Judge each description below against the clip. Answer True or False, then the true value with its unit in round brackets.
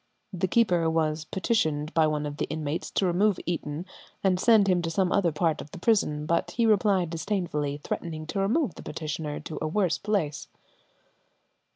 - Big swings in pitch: False (4.1 semitones)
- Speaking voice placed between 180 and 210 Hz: False (170 Hz)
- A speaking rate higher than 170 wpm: True (180 wpm)